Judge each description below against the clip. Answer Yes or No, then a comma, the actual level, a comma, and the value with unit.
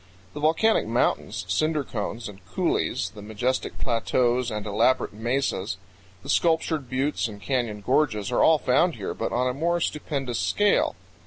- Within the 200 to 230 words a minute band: No, average, 155 wpm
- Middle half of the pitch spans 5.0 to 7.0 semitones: Yes, wide, 5.6 semitones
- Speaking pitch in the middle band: No, low, 125 Hz